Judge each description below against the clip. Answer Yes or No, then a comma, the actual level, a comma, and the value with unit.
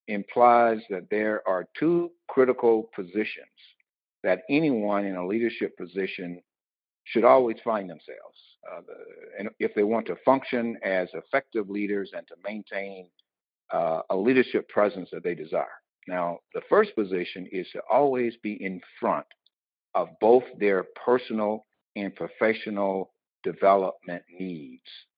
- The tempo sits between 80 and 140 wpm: Yes, slow, 135 wpm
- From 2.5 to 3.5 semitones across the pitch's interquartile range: No, average, 4.3 semitones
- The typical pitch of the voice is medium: No, low, 105 Hz